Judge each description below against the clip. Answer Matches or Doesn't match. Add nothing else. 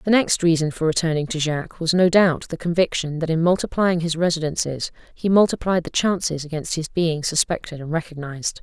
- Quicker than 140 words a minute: Matches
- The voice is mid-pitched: Matches